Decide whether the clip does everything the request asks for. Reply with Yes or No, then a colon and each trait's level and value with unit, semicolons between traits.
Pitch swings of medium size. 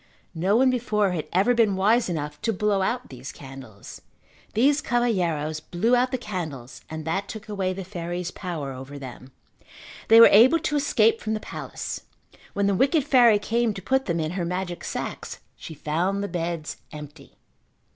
No: wide, 6.2 semitones